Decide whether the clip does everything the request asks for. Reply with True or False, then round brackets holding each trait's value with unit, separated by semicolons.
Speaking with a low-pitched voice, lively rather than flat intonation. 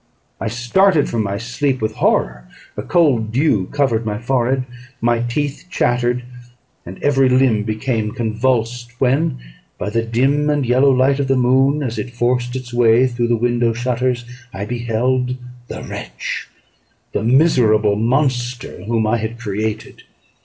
False (120 Hz; 2.5 semitones)